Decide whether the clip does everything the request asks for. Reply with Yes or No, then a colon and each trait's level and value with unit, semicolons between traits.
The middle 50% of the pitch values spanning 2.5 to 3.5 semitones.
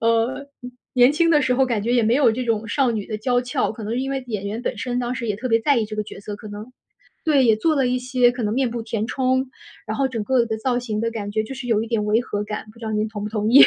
Yes: average, 2.8 semitones